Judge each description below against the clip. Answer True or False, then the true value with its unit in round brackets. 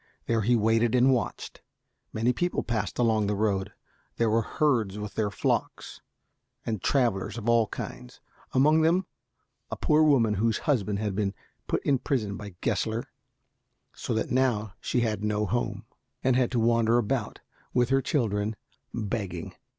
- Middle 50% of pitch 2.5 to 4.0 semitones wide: True (2.9 semitones)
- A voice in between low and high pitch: False (115 Hz)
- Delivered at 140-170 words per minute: True (160 wpm)